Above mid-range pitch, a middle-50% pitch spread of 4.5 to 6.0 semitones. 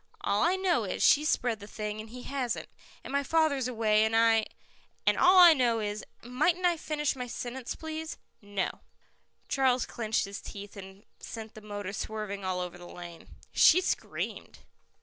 Yes: high, 230 Hz; wide, 5.4 semitones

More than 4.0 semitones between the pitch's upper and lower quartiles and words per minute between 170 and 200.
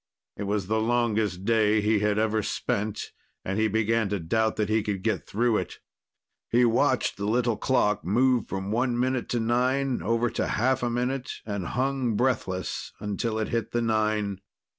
No: average, 2.7 semitones; average, 180 wpm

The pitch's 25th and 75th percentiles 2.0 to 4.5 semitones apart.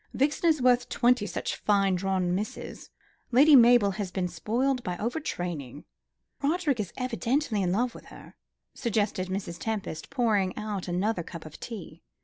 No: average, 5.2 semitones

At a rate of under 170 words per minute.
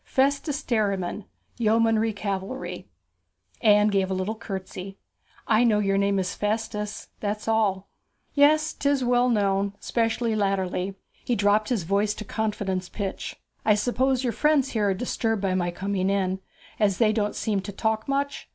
Yes: average, 155 wpm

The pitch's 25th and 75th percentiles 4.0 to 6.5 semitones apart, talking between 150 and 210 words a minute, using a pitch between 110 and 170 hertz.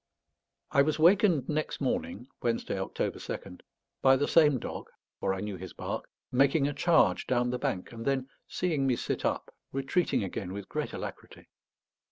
Yes: average, 5.2 semitones; average, 170 wpm; low, 135 Hz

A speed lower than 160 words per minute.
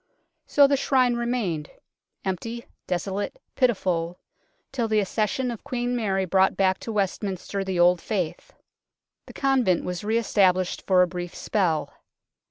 Yes: average, 140 wpm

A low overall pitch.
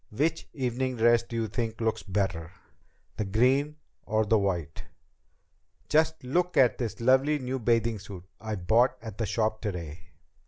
Yes: low, 115 Hz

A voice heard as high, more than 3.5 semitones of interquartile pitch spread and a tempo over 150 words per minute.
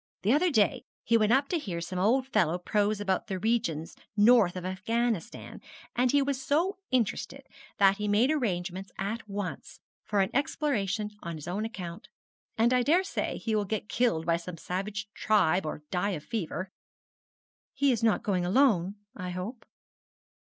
Yes: high, 210 Hz; average, 4.7 semitones; average, 170 wpm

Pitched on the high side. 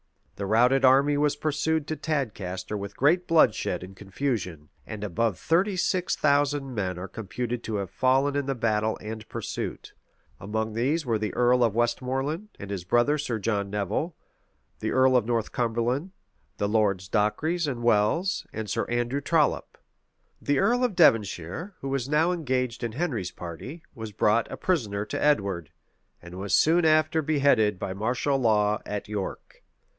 No: low, 120 Hz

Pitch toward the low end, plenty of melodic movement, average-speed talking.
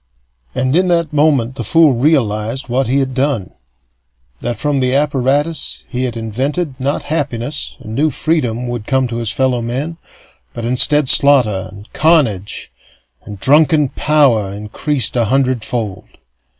No: low, 130 Hz; average, 4.1 semitones; average, 145 wpm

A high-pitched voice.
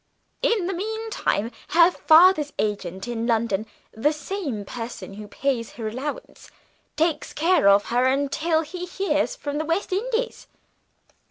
Yes: very high, 295 Hz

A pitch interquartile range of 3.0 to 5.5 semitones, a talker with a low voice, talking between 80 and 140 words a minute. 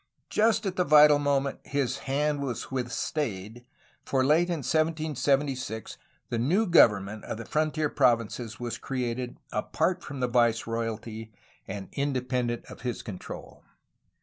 Yes: average, 4.3 semitones; low, 130 Hz; slow, 135 wpm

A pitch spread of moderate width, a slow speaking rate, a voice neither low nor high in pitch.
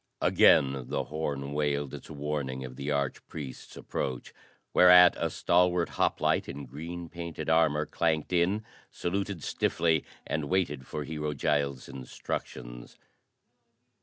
No: average, 3.5 semitones; slow, 125 wpm; very low, 75 Hz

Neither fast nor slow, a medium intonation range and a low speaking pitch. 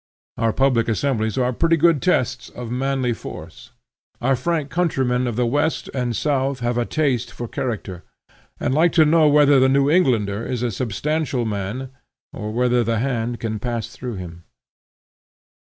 Yes: average, 165 wpm; average, 3.3 semitones; low, 125 Hz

